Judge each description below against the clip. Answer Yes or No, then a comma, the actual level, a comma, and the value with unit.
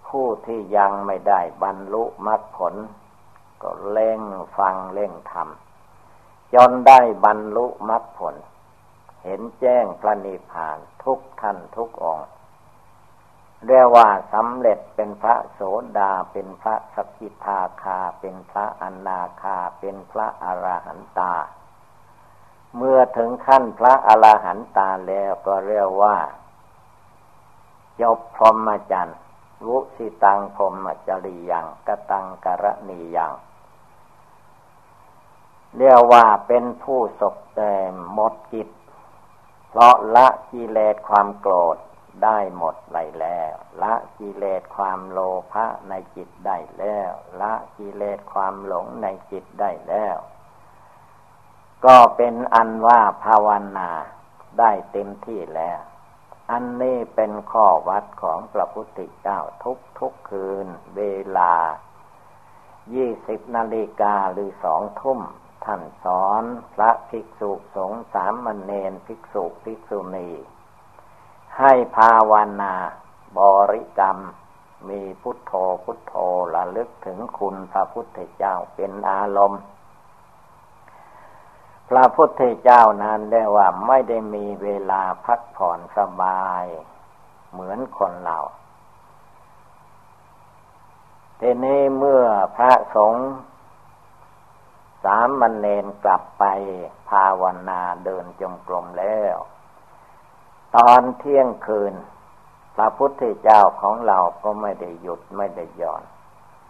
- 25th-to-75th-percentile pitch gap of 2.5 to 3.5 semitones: Yes, average, 3.2 semitones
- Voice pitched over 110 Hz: No, low, 105 Hz